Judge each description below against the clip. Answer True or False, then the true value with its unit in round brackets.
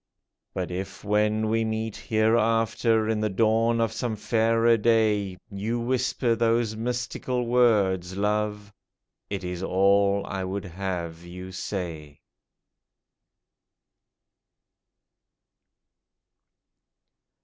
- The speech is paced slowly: True (95 wpm)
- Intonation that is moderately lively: True (3.0 semitones)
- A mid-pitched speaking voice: False (105 Hz)